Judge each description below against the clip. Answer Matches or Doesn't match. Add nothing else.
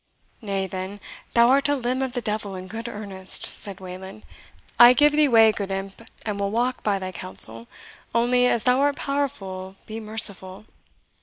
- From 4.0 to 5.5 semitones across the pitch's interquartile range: Matches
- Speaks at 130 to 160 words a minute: Doesn't match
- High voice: Matches